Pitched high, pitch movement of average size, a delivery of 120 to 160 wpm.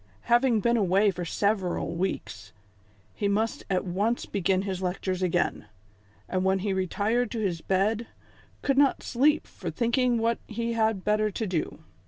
Yes: high, 205 Hz; average, 3.7 semitones; average, 155 wpm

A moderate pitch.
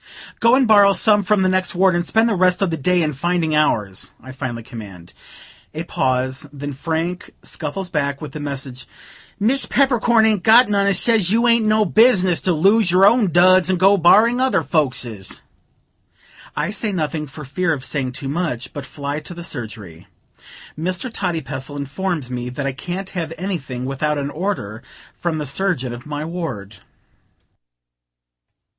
Yes: medium, 165 Hz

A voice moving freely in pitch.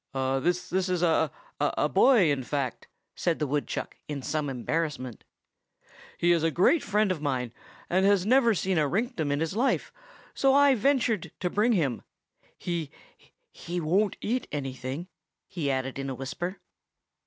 Yes: wide, 6.0 semitones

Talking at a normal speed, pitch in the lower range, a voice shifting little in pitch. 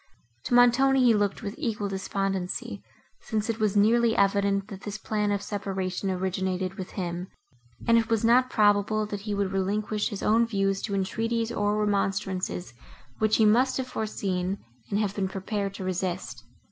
No: average, 170 wpm; high, 205 Hz; narrow, 2.2 semitones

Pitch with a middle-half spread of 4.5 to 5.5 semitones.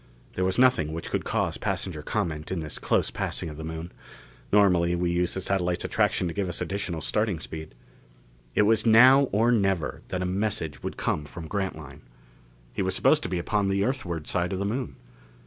No: average, 3.9 semitones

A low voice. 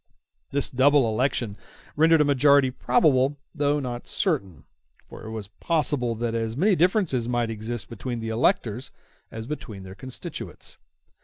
Yes: low, 125 Hz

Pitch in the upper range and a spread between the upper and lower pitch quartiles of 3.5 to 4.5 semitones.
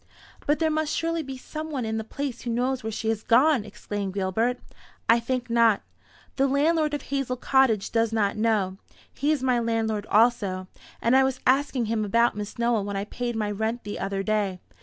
Yes: high, 235 Hz; average, 3.8 semitones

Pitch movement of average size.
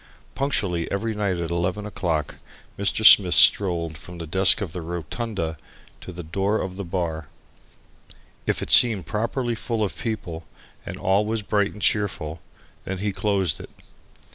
Yes: average, 3.6 semitones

